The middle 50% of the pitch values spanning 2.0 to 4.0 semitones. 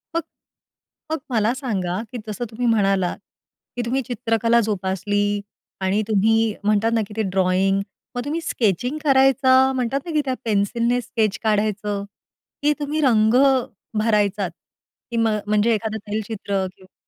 Yes: average, 3.3 semitones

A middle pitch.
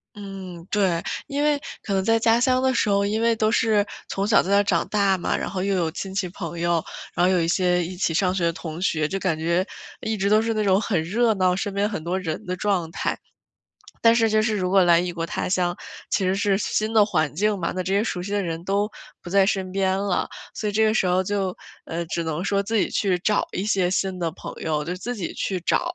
No: high, 195 Hz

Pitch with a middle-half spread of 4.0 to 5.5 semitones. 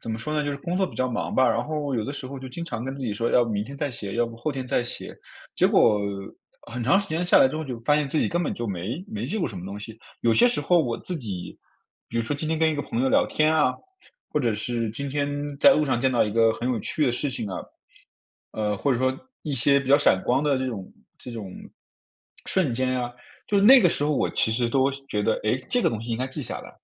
Yes: average, 4.4 semitones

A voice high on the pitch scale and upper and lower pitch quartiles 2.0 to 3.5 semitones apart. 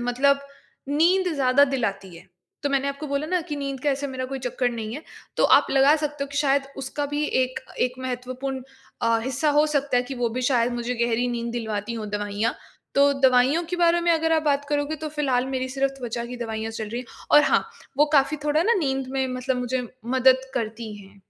Yes: very high, 265 Hz; average, 2.9 semitones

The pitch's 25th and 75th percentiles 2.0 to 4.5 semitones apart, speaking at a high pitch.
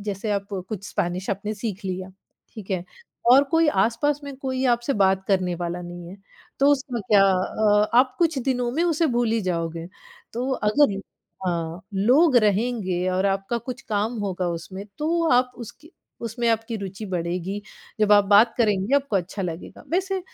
No: average, 5.0 semitones; high, 210 Hz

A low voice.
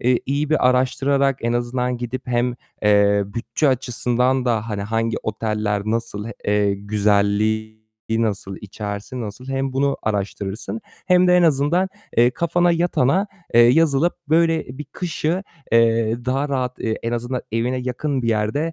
Yes: low, 120 Hz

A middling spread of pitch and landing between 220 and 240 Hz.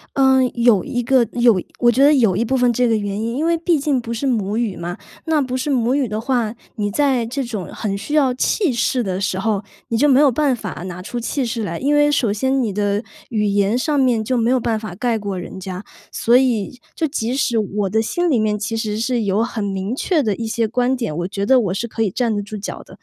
Yes: average, 4.0 semitones; high, 230 Hz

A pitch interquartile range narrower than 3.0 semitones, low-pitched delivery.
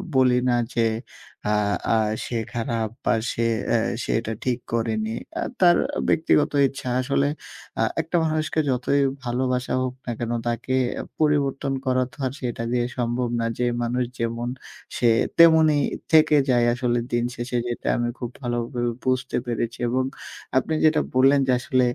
Yes: narrow, 2.4 semitones; low, 125 Hz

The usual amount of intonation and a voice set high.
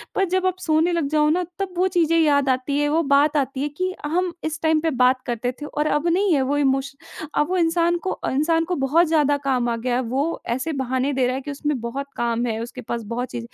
Yes: average, 4.1 semitones; very high, 290 Hz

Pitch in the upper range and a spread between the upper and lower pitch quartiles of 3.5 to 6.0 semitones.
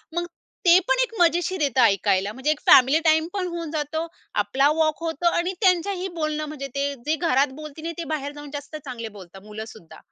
Yes: very high, 305 Hz; average, 4.0 semitones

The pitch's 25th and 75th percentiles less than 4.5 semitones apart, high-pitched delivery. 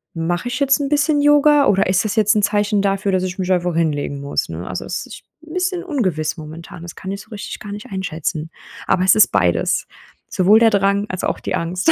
No: average, 5.0 semitones; high, 195 Hz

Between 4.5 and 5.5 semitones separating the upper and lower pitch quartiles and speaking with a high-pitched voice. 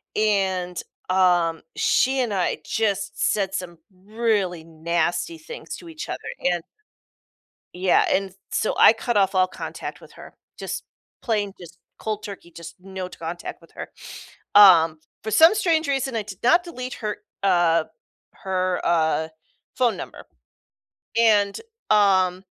No: average, 3.9 semitones; high, 195 Hz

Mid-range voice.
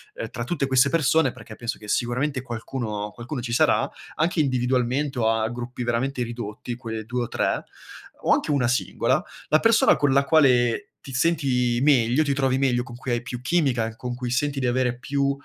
No: low, 125 Hz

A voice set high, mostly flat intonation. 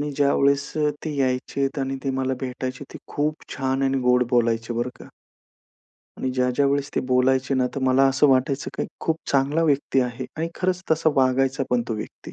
No: low, 135 Hz; narrow, 1.7 semitones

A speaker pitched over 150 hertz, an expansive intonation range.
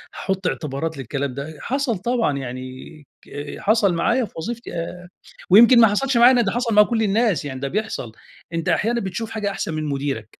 Yes: high, 190 Hz; wide, 7.9 semitones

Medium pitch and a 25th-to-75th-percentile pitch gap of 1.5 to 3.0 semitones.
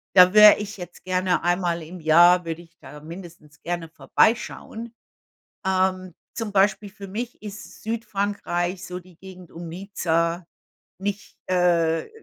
Yes: medium, 180 Hz; average, 2.7 semitones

